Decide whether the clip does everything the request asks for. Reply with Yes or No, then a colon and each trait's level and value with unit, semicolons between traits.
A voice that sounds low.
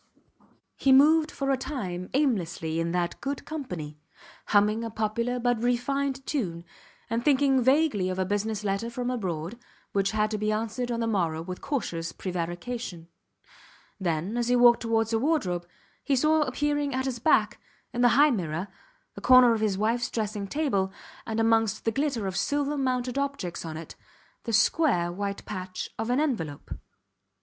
No: high, 225 Hz